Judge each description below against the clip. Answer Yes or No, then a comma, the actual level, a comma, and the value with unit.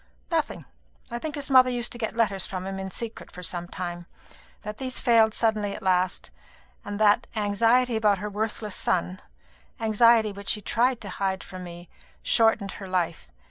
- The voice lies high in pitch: Yes, high, 210 Hz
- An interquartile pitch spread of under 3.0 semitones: No, average, 3.4 semitones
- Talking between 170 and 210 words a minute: Yes, average, 180 wpm